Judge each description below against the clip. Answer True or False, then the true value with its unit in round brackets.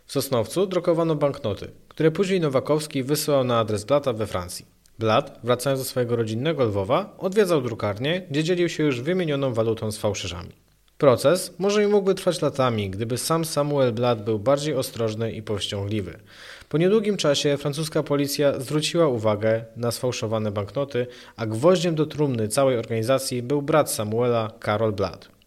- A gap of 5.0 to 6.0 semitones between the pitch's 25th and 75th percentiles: True (5.6 semitones)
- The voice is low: True (130 Hz)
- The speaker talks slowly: False (155 wpm)